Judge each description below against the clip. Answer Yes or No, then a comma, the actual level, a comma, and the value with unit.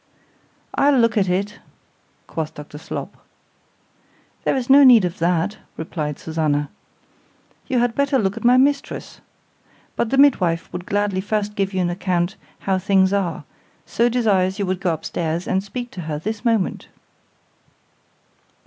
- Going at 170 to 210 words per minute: No, average, 145 wpm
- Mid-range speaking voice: No, high, 195 Hz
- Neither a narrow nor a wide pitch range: Yes, average, 4.9 semitones